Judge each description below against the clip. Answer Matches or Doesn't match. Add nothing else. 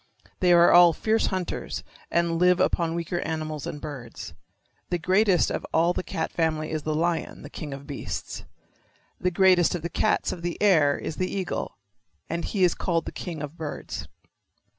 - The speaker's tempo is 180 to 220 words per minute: Matches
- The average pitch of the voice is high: Doesn't match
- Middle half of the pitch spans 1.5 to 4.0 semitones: Matches